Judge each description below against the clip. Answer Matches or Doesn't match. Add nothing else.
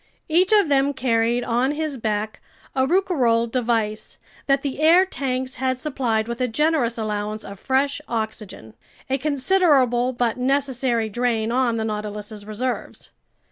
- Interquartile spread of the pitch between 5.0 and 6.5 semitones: Doesn't match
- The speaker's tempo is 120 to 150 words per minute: Matches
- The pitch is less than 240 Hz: Doesn't match